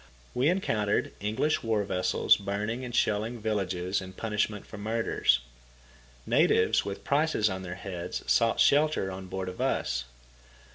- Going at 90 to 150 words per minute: Yes, average, 140 wpm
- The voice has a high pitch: No, low, 105 Hz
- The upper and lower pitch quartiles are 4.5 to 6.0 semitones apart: No, average, 3.4 semitones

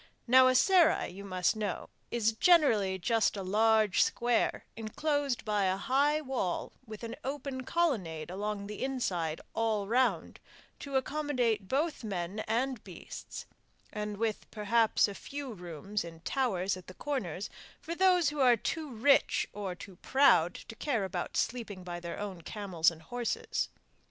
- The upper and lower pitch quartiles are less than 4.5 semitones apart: No, wide, 5.6 semitones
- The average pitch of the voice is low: No, high, 220 Hz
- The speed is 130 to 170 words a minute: Yes, average, 155 wpm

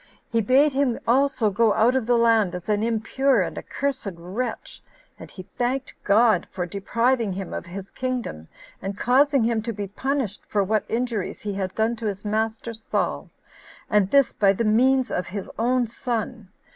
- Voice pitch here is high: Yes, high, 225 Hz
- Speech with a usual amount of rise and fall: Yes, average, 3.8 semitones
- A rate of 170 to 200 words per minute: Yes, average, 180 wpm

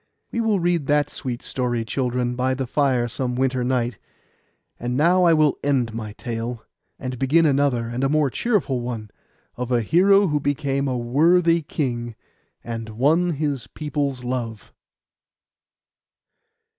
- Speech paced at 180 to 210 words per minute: No, average, 145 wpm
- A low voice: Yes, low, 130 Hz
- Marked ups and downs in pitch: No, average, 3.8 semitones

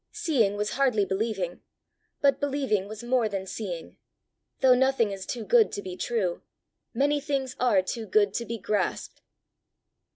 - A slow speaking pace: No, average, 155 wpm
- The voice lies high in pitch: Yes, high, 225 Hz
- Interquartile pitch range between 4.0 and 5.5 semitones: Yes, average, 4.9 semitones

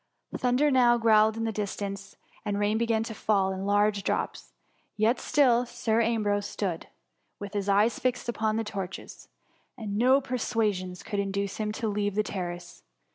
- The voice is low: No, high, 215 Hz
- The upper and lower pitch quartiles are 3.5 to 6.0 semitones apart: No, narrow, 2.5 semitones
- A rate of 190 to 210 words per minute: No, average, 170 wpm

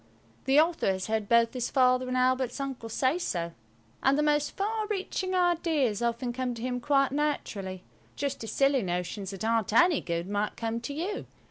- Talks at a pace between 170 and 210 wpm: Yes, average, 180 wpm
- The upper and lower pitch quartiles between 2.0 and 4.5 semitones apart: No, average, 5.0 semitones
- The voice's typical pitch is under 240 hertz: No, very high, 255 Hz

